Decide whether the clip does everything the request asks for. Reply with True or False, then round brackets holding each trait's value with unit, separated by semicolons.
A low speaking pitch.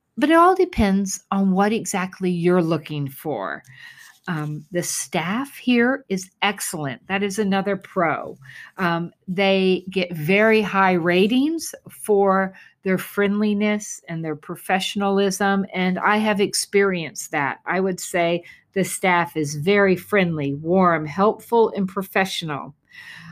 False (190 Hz)